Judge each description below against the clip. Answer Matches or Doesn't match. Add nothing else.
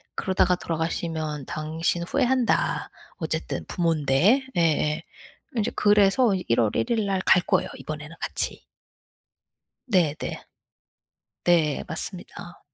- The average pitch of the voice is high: Doesn't match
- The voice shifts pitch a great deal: Doesn't match